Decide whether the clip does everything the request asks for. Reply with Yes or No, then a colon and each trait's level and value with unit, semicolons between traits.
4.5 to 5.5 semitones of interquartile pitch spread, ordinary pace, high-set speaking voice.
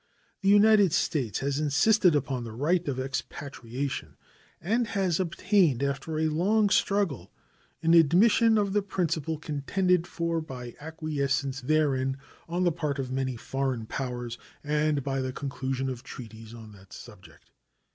No: average, 5.0 semitones; average, 145 wpm; medium, 145 Hz